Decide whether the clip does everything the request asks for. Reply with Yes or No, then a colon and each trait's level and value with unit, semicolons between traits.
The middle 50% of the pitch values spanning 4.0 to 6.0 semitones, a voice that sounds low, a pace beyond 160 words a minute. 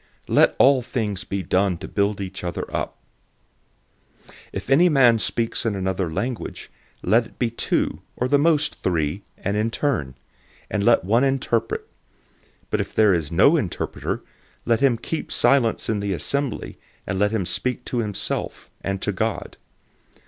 Yes: average, 4.5 semitones; low, 110 Hz; average, 170 wpm